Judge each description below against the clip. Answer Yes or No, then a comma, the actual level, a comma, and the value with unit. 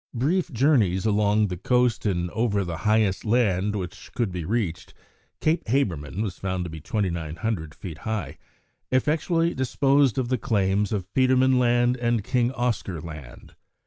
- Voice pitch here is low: Yes, low, 110 Hz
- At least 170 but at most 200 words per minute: No, average, 150 wpm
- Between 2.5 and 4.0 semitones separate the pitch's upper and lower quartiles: No, average, 5.2 semitones